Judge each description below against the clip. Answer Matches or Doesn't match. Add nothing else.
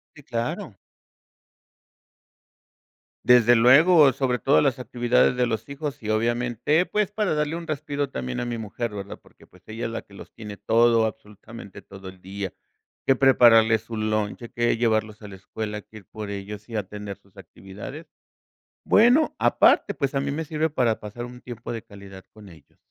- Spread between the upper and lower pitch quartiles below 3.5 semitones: Doesn't match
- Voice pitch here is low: Matches